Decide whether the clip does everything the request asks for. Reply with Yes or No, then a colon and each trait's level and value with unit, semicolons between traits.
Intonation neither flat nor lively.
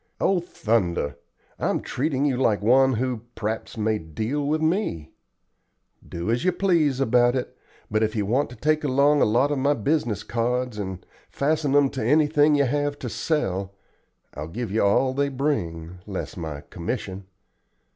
No: wide, 5.7 semitones